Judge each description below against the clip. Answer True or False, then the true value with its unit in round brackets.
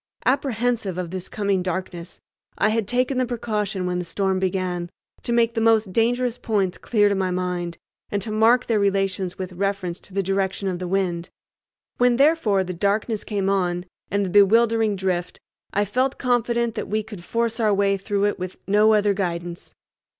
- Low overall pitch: False (200 Hz)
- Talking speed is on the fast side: False (185 wpm)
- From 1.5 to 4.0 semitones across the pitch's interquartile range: True (3.4 semitones)